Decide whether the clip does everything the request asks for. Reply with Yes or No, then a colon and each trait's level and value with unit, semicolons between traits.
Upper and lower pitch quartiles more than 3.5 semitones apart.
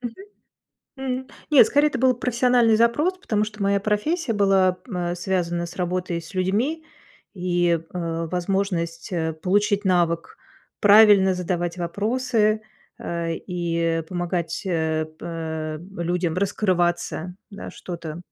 Yes: average, 4.0 semitones